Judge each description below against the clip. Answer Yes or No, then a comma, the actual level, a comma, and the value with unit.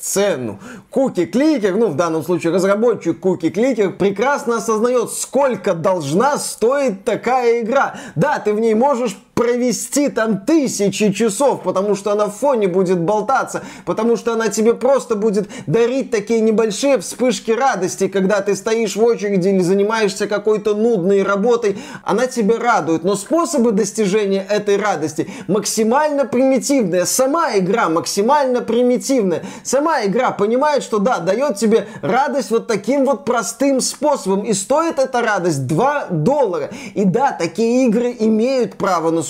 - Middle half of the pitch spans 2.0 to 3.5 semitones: No, average, 4.1 semitones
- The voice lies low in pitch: No, high, 225 Hz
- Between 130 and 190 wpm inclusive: Yes, average, 145 wpm